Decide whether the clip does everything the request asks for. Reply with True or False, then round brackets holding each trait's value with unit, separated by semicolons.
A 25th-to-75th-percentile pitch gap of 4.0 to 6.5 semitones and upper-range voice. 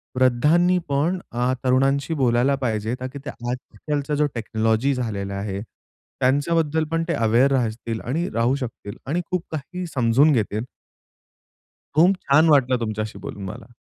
False (4.5 semitones; 130 Hz)